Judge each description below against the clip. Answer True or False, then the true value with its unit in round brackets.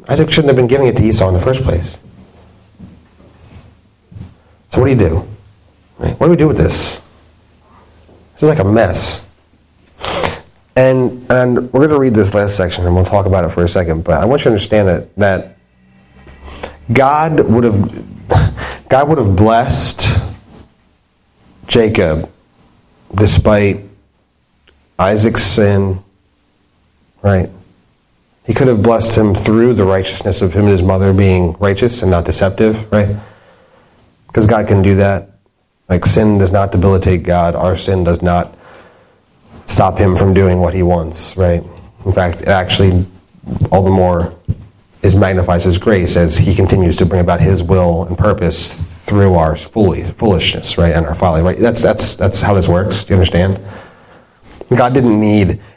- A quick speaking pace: False (160 wpm)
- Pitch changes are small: False (3.1 semitones)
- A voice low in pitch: True (95 Hz)